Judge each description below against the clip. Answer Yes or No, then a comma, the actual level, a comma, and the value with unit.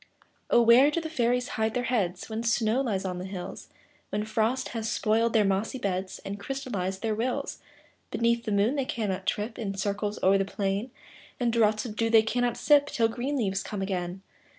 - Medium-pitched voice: No, high, 220 Hz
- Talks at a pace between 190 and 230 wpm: Yes, average, 195 wpm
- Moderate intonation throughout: Yes, average, 3.3 semitones